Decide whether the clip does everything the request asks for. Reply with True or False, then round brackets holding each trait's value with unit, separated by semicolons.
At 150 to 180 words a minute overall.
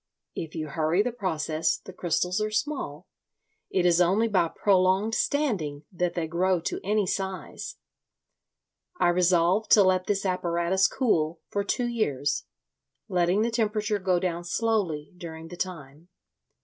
False (140 wpm)